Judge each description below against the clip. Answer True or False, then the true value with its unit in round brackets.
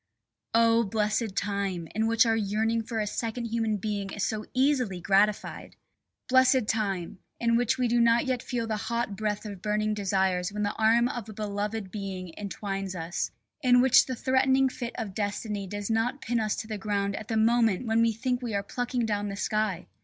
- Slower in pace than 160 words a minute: False (200 wpm)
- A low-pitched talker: False (215 Hz)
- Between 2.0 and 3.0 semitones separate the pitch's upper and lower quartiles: True (2.5 semitones)